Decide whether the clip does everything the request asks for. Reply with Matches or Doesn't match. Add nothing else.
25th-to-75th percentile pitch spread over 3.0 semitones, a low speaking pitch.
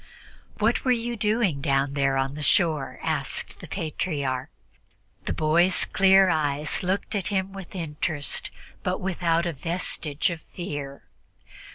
Doesn't match